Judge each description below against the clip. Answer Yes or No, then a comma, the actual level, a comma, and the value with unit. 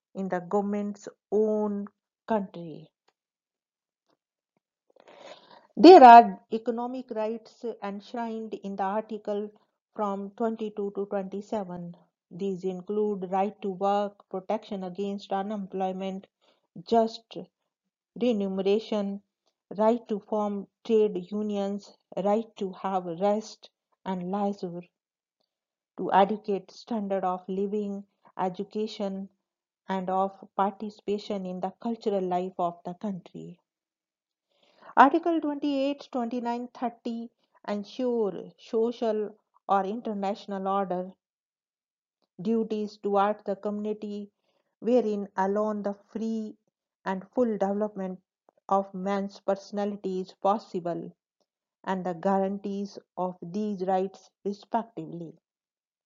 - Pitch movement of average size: No, narrow, 2.1 semitones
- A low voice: No, high, 200 Hz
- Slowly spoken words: Yes, slow, 90 wpm